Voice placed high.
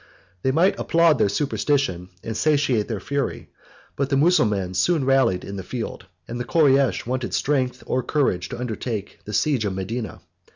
No: low, 125 Hz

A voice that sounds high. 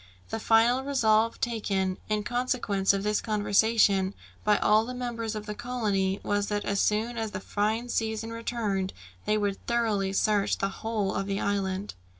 Yes: high, 210 Hz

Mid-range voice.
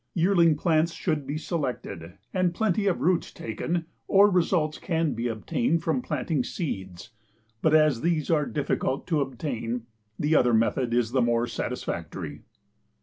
Yes: medium, 150 Hz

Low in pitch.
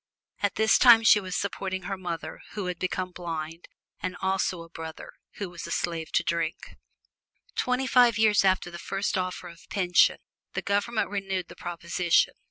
No: medium, 185 Hz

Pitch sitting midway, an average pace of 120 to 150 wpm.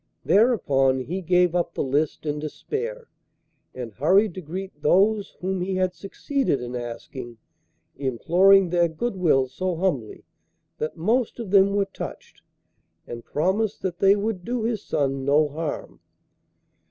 Yes: medium, 180 Hz; average, 140 wpm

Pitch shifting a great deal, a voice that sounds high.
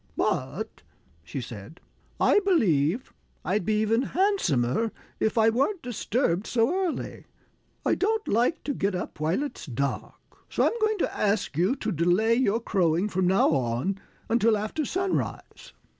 Yes: wide, 7.7 semitones; high, 215 Hz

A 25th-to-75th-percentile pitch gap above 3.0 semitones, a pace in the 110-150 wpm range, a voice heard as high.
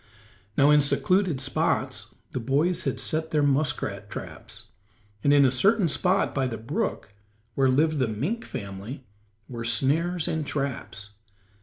No: average, 4.3 semitones; average, 145 wpm; medium, 140 Hz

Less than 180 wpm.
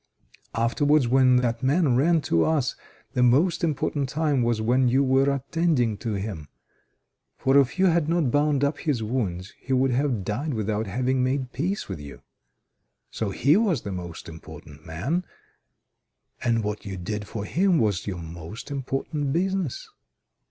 Yes: average, 160 wpm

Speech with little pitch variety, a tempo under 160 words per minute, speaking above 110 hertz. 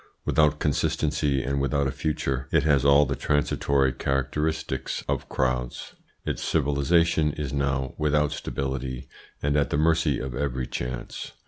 No: narrow, 2.0 semitones; average, 140 wpm; very low, 70 Hz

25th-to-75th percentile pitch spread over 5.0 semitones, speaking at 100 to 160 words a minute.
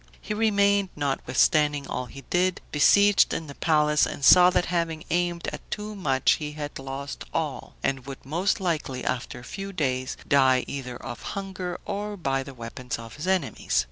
No: wide, 5.5 semitones; average, 175 wpm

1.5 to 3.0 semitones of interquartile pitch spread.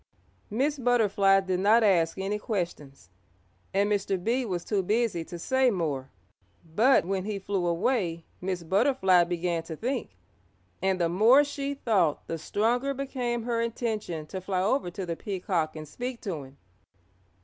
No: average, 5.2 semitones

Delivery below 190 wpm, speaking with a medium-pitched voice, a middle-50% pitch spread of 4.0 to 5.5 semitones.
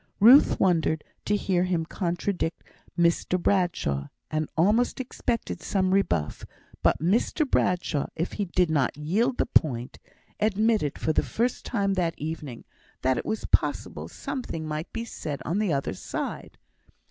Yes: average, 145 wpm; medium, 175 Hz; average, 5.1 semitones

